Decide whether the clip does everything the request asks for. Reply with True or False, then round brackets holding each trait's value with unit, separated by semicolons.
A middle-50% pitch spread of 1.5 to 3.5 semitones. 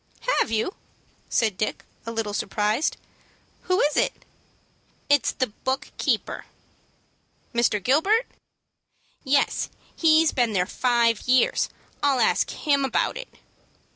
False (4.7 semitones)